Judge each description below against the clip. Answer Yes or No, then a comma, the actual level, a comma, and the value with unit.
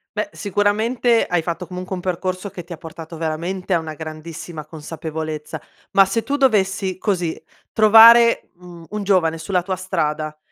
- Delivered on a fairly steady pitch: No, average, 3.8 semitones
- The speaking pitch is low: No, medium, 180 Hz